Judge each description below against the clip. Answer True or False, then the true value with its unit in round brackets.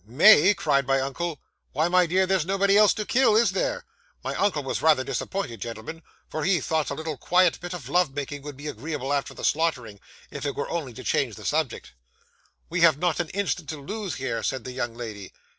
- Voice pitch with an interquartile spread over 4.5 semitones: True (5.0 semitones)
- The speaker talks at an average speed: False (215 wpm)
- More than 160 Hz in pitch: False (155 Hz)